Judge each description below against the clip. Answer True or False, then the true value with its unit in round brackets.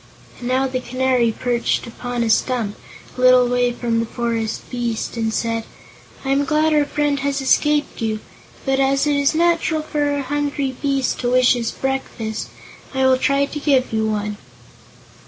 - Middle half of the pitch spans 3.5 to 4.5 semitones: False (3.1 semitones)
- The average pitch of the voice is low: False (255 Hz)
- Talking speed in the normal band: True (175 wpm)